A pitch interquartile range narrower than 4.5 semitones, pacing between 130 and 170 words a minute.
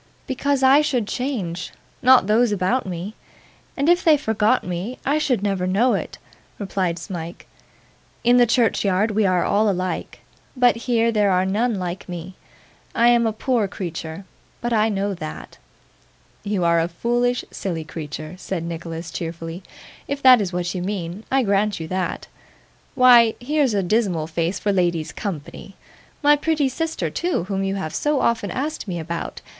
No: wide, 5.5 semitones; average, 165 wpm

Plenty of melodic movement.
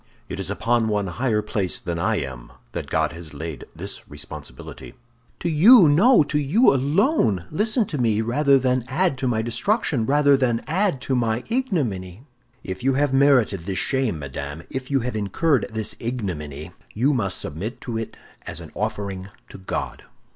Yes: wide, 7.1 semitones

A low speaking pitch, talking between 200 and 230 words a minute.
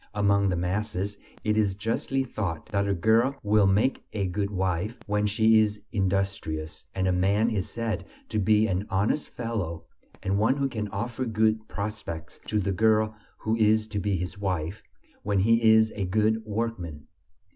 No: low, 105 Hz; average, 175 wpm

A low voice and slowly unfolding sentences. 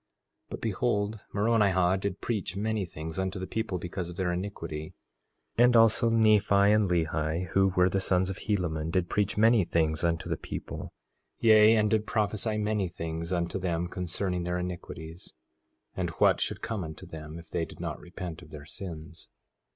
No: very low, 95 Hz; average, 175 wpm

